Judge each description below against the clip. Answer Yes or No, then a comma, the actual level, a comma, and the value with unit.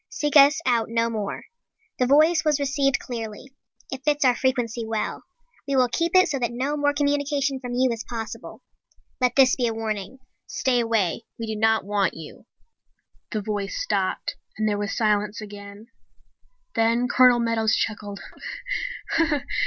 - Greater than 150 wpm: Yes, average, 160 wpm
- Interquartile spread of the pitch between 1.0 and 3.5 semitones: No, average, 4.0 semitones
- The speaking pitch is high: Yes, high, 235 Hz